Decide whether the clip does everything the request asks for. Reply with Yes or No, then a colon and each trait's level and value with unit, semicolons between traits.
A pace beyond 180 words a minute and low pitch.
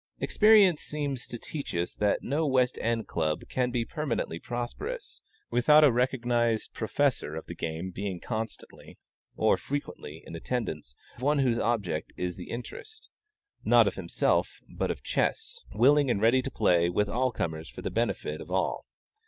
No: average, 160 wpm; low, 120 Hz